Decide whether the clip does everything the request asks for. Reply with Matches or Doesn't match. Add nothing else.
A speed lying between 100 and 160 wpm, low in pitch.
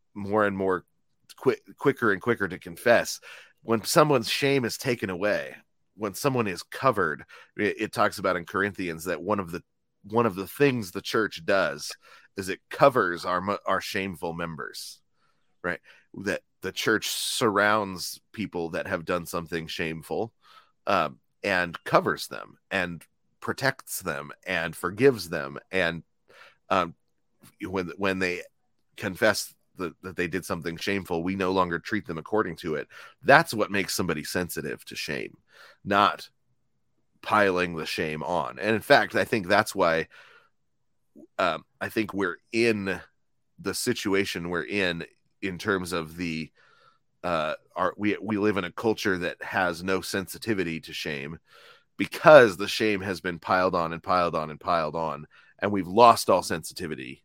Matches